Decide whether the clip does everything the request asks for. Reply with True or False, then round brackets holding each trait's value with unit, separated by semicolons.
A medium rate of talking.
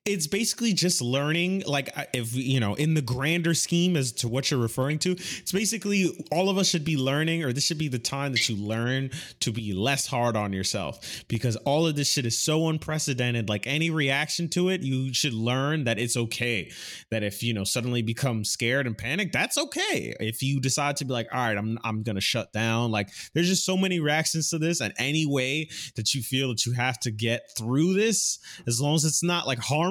False (225 wpm)